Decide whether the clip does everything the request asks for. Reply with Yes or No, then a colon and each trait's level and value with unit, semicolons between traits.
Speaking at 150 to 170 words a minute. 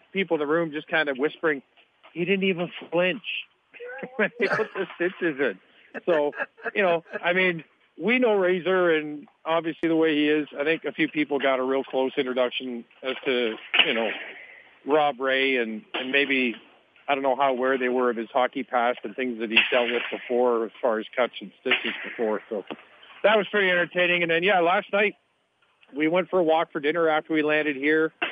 No: fast, 205 wpm